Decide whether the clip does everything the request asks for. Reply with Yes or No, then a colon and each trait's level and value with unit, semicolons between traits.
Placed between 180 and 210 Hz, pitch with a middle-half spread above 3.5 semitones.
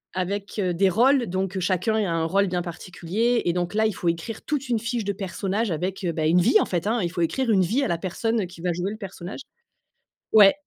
Yes: high, 190 Hz; average, 3.9 semitones